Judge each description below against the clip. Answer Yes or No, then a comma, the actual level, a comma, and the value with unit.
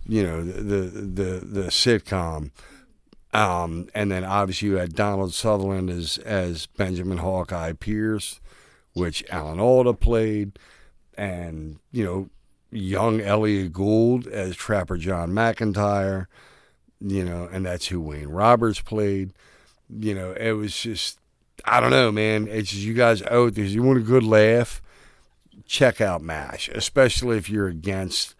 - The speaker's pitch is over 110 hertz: No, low, 100 Hz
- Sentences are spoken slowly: No, average, 145 wpm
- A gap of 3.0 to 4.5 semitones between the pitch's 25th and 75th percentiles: Yes, average, 3.4 semitones